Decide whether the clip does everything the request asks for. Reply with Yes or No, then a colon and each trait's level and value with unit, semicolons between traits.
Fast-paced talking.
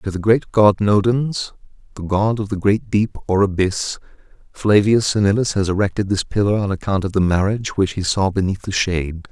No: average, 195 wpm